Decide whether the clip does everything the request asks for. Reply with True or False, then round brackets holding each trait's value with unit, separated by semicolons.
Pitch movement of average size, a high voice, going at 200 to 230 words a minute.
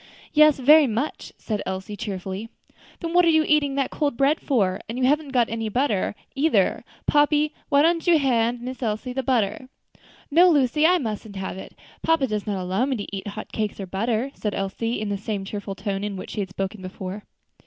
False (6.0 semitones; 230 Hz; 205 wpm)